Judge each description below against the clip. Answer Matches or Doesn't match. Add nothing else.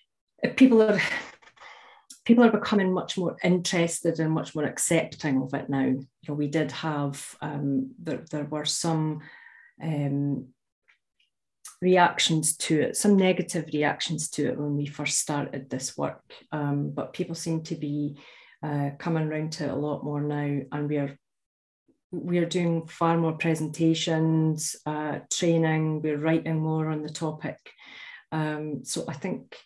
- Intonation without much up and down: Matches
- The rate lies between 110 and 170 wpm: Matches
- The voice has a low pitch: Doesn't match